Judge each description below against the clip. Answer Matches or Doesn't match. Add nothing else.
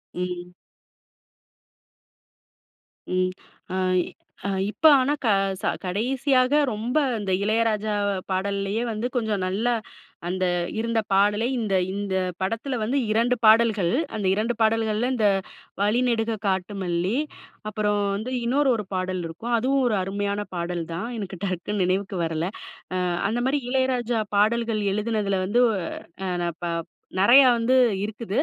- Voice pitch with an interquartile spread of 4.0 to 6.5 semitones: Doesn't match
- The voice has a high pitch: Matches